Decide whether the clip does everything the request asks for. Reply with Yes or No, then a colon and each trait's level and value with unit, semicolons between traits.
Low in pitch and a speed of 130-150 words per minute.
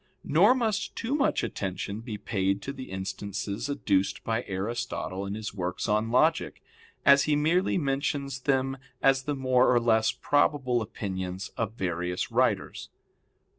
Yes: low, 120 Hz; average, 145 wpm